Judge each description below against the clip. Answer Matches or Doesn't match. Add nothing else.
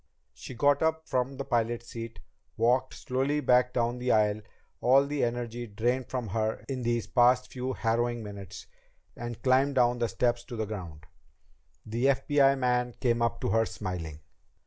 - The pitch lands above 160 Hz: Doesn't match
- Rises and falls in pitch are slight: Matches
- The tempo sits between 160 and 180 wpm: Matches